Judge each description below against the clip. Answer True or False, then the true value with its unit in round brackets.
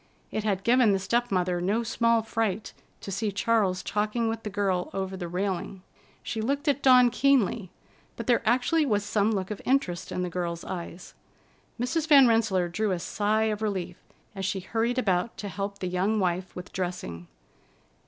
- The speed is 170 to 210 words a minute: True (185 wpm)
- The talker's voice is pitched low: False (205 Hz)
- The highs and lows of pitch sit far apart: False (3.9 semitones)